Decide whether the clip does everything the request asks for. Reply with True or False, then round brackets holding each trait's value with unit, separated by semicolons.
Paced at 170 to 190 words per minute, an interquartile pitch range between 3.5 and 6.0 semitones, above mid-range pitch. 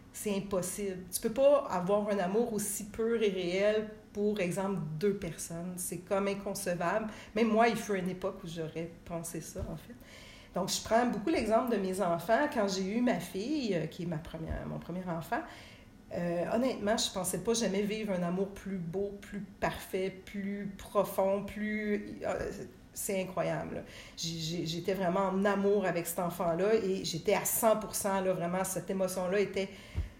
False (175 wpm; 2.9 semitones; 195 Hz)